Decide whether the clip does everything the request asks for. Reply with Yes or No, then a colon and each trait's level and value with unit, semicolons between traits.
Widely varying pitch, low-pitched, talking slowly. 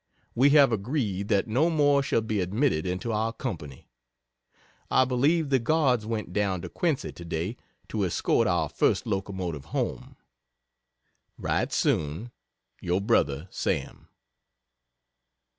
Yes: wide, 6.3 semitones; low, 110 Hz; slow, 125 wpm